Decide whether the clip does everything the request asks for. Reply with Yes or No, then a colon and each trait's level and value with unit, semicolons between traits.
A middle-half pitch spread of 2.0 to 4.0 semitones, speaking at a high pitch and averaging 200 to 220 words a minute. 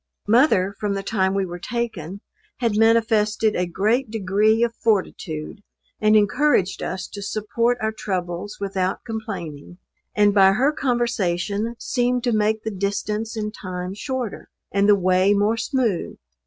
No: average, 3.0 semitones; high, 210 Hz; average, 145 wpm